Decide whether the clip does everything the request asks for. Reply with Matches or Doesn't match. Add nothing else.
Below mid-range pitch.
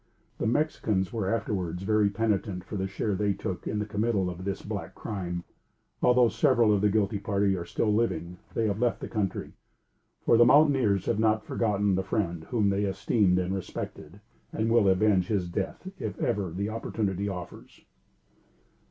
Matches